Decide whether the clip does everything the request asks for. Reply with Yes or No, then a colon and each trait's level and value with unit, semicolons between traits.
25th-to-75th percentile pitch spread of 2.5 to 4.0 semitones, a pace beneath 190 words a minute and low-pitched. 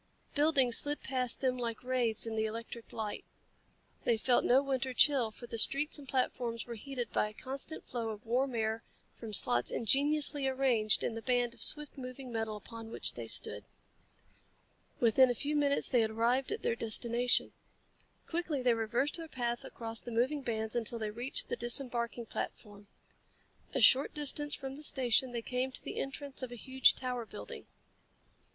No: average, 2.9 semitones; average, 180 wpm; high, 245 Hz